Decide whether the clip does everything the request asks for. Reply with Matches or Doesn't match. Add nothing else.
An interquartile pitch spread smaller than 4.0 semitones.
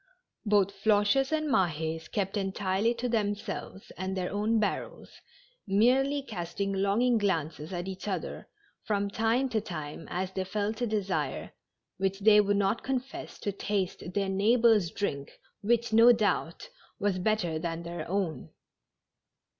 Matches